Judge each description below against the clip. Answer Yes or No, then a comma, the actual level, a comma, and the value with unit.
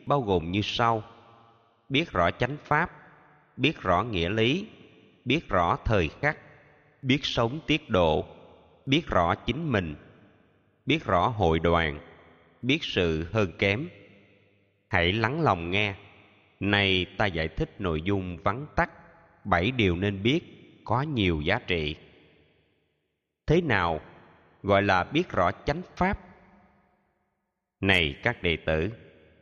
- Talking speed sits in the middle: No, slow, 130 wpm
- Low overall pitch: Yes, low, 100 Hz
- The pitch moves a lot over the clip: Yes, wide, 8.1 semitones